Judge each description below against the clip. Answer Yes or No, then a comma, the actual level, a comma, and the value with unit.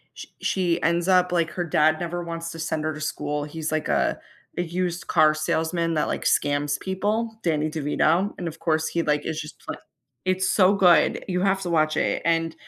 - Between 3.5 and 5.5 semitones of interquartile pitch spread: No, narrow, 2.5 semitones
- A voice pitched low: No, medium, 165 Hz